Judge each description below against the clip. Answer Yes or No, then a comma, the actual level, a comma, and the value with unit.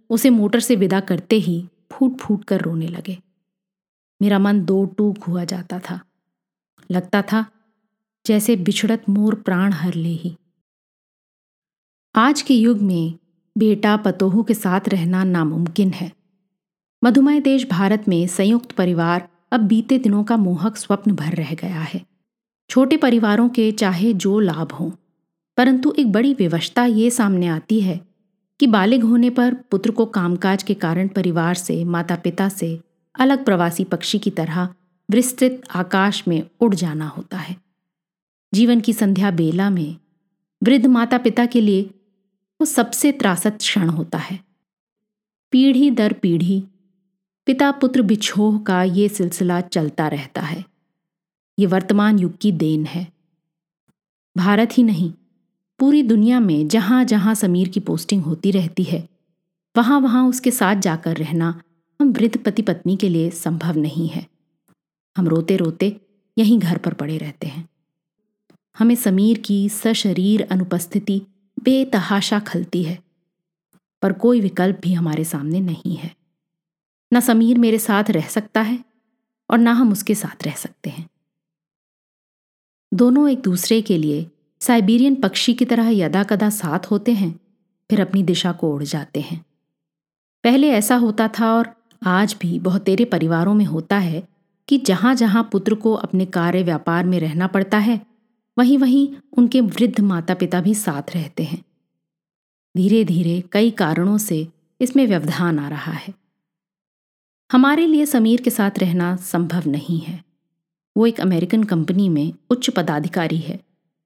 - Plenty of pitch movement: No, average, 4.2 semitones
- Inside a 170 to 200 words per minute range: No, average, 150 wpm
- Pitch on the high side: Yes, high, 195 Hz